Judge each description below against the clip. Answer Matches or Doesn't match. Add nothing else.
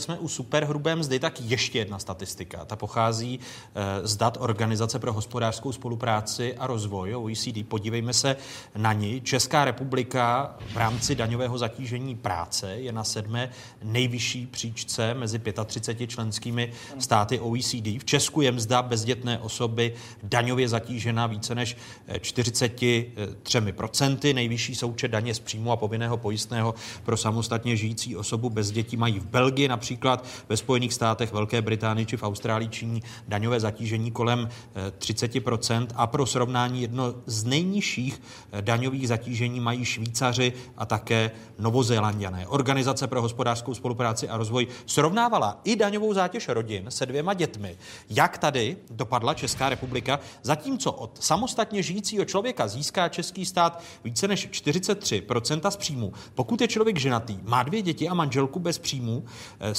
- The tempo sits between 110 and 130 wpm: Doesn't match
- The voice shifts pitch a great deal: Doesn't match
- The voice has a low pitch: Matches